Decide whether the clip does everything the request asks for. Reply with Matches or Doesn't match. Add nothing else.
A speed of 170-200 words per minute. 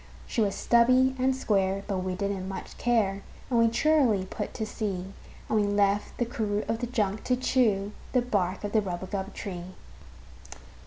Matches